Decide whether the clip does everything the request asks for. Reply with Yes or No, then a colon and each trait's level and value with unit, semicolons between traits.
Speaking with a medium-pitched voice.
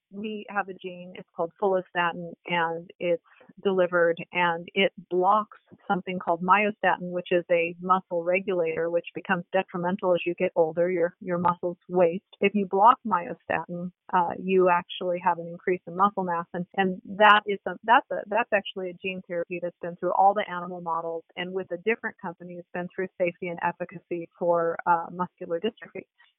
Yes: medium, 180 Hz